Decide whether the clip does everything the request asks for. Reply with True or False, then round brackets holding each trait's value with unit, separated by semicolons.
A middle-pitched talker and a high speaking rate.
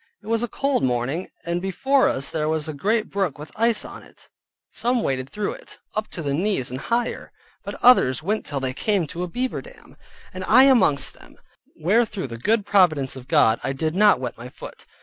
True (180 Hz; 215 wpm)